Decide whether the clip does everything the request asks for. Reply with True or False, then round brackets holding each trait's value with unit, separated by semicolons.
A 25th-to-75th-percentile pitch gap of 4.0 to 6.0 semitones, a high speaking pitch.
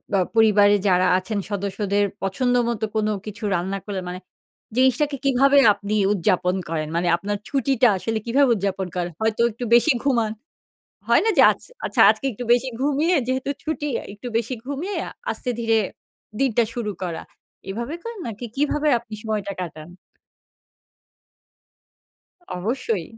True (4.9 semitones; 220 Hz)